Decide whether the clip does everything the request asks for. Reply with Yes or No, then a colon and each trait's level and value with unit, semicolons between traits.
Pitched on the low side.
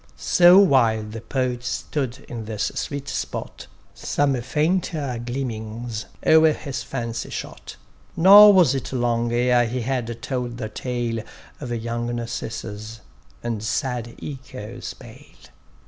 Yes: low, 120 Hz